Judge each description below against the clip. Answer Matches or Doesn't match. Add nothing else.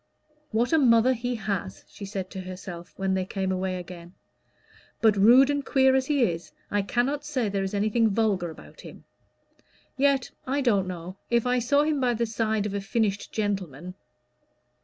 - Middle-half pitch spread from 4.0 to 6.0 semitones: Matches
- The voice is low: Doesn't match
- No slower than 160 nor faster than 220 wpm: Matches